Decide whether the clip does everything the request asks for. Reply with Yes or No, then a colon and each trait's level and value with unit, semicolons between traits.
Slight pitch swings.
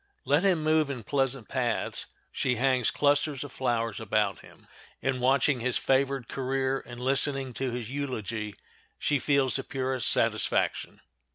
Yes: narrow, 2.3 semitones